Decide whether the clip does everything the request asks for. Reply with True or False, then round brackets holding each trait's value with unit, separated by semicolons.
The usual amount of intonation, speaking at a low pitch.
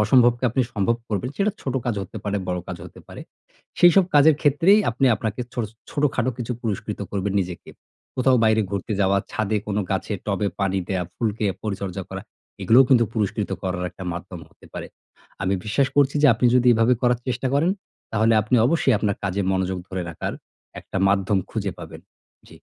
True (4.6 semitones; 110 Hz)